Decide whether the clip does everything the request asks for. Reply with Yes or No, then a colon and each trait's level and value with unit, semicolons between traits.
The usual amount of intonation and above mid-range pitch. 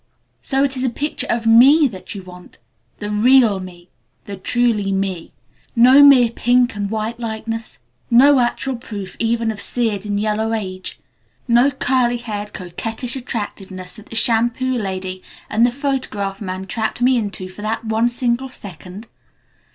Yes: average, 3.4 semitones; high, 225 Hz